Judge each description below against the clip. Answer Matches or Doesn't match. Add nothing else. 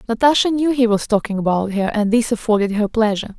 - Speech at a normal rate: Doesn't match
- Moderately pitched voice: Doesn't match